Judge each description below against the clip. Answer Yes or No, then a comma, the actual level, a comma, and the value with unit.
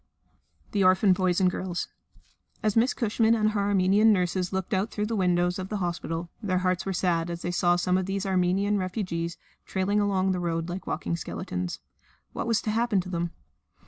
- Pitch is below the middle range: No, medium, 185 Hz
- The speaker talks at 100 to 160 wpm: No, average, 195 wpm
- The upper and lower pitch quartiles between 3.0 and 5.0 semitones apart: No, narrow, 2.4 semitones